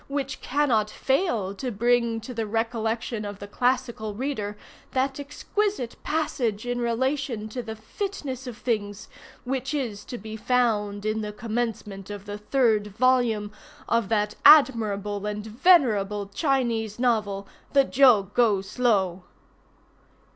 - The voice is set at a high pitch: Yes, high, 225 Hz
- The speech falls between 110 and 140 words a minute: Yes, slow, 135 wpm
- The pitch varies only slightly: No, average, 3.7 semitones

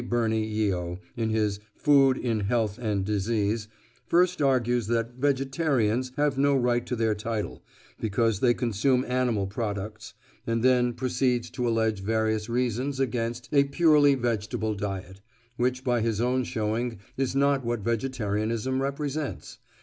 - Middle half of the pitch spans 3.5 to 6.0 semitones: No, average, 3.1 semitones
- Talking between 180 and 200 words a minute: No, average, 140 wpm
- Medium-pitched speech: No, low, 120 Hz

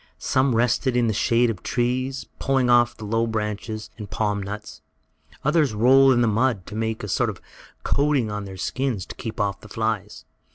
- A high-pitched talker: No, low, 115 Hz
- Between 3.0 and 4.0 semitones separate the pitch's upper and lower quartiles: Yes, average, 3.3 semitones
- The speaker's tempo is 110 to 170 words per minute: No, average, 200 wpm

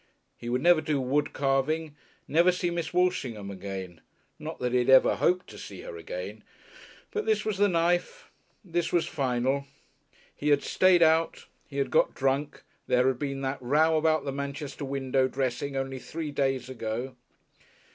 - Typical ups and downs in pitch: Yes, average, 4.1 semitones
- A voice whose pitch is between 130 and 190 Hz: Yes, medium, 140 Hz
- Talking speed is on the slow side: No, average, 170 wpm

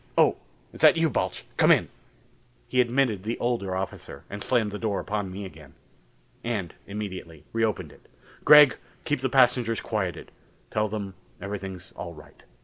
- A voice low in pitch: Yes, low, 105 Hz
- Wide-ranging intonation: No, average, 4.1 semitones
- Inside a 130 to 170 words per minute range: Yes, average, 155 wpm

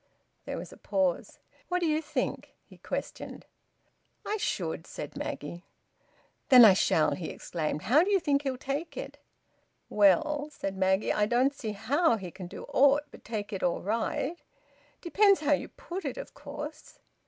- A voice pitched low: No, very high, 255 Hz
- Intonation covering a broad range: Yes, wide, 7.9 semitones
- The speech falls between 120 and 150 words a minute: No, average, 165 wpm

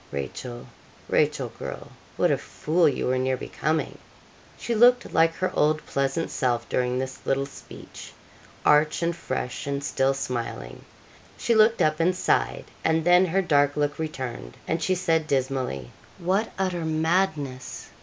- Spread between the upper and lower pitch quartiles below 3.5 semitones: No, average, 4.6 semitones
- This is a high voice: No, medium, 150 Hz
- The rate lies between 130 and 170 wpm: Yes, average, 150 wpm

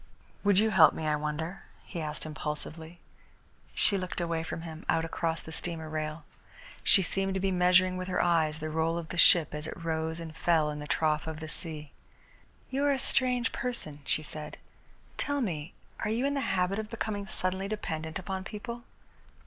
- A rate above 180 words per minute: Yes, average, 195 wpm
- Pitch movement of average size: Yes, average, 3.6 semitones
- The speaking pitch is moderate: Yes, medium, 170 Hz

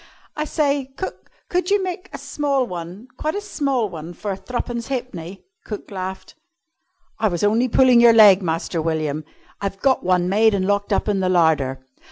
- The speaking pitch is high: Yes, high, 205 Hz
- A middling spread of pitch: No, wide, 6.6 semitones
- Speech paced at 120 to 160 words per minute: No, average, 180 wpm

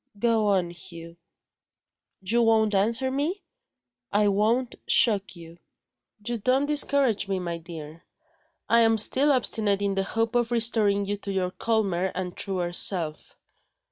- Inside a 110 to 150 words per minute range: Yes, average, 140 wpm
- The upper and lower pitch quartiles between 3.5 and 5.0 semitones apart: Yes, average, 4.0 semitones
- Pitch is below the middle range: No, high, 205 Hz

